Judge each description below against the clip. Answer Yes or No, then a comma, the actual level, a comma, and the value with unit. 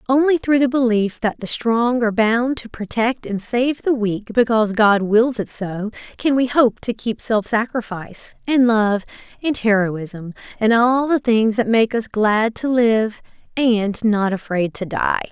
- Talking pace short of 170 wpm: No, average, 180 wpm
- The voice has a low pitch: No, high, 225 Hz